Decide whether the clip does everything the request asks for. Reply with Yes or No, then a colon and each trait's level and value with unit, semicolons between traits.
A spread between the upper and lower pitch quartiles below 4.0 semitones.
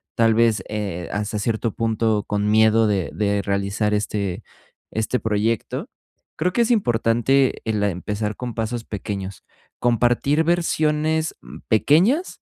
Yes: average, 3.2 semitones